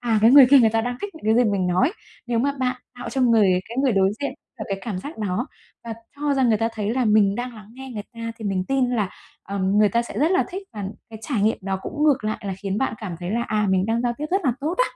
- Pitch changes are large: No, average, 4.2 semitones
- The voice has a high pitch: Yes, high, 230 Hz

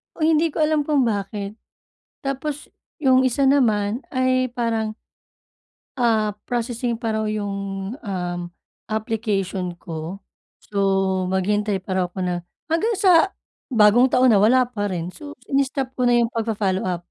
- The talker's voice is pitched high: Yes, high, 225 Hz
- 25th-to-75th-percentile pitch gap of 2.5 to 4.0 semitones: No, average, 4.6 semitones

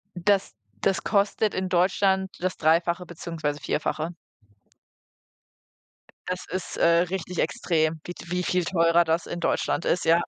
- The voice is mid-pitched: Yes, medium, 175 Hz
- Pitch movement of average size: No, narrow, 1.8 semitones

